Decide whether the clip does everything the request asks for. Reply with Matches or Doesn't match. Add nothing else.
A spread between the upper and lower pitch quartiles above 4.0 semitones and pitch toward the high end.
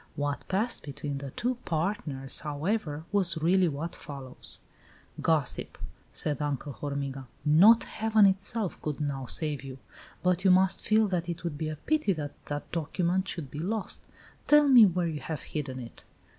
Doesn't match